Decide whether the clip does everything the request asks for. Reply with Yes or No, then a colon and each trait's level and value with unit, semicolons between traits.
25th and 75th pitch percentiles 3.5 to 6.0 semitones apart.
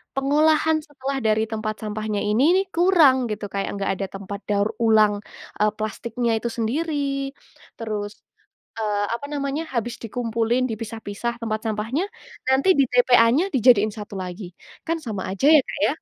Yes: average, 3.9 semitones